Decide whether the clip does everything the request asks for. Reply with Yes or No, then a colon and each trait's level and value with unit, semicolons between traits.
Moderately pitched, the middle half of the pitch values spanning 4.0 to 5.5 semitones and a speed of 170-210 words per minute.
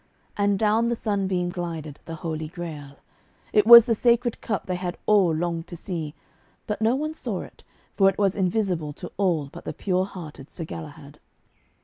Yes: medium, 180 Hz; average, 4.4 semitones; average, 180 wpm